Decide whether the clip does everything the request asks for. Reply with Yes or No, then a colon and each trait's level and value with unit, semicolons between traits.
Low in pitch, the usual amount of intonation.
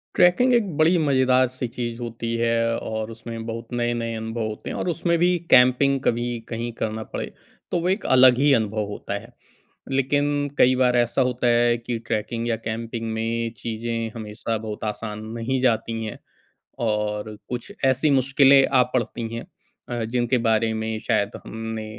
No: low, 115 Hz; narrow, 2.3 semitones